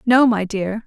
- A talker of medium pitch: No, high, 220 Hz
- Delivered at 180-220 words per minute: Yes, fast, 210 wpm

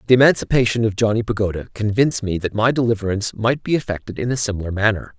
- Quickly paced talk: No, average, 195 wpm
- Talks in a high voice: No, low, 110 Hz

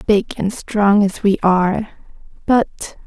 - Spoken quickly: No, slow, 135 wpm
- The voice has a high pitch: Yes, high, 205 Hz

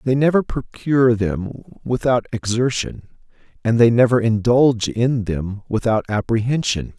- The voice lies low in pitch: Yes, low, 115 Hz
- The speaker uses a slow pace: Yes, slow, 120 wpm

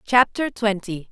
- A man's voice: No, female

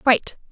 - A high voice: Yes, high, 245 Hz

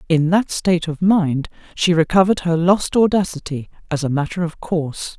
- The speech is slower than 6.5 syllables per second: Yes, 5.3 syllables/s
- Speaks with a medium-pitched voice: Yes, medium, 170 Hz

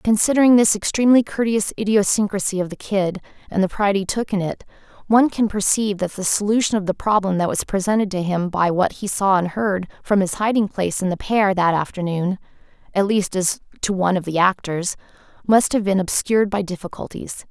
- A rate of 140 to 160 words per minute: No, average, 200 wpm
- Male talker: No, female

